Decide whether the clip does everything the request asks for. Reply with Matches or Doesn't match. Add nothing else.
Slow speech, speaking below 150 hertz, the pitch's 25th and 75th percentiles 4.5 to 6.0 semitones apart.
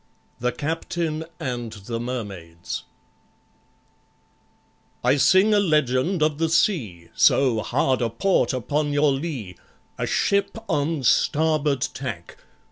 Matches